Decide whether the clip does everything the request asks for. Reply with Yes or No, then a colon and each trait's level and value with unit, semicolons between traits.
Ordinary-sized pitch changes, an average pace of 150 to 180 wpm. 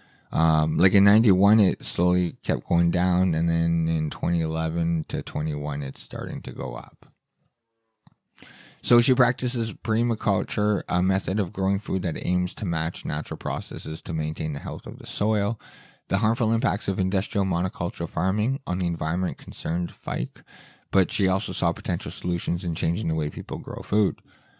Yes: average, 4.1 semitones; average, 165 wpm